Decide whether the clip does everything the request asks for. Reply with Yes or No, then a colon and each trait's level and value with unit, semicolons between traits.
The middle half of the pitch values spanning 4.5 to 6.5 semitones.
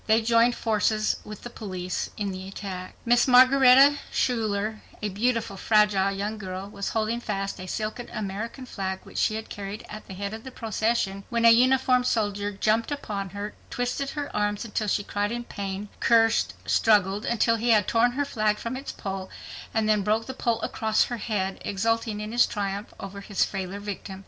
No: average, 2.7 semitones